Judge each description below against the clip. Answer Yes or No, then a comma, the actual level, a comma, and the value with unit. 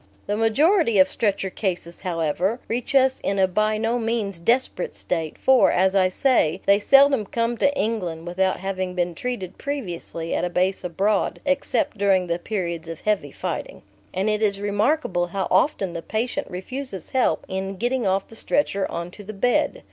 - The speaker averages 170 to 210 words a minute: Yes, average, 180 wpm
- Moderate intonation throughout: Yes, average, 4.4 semitones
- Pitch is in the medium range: No, high, 200 Hz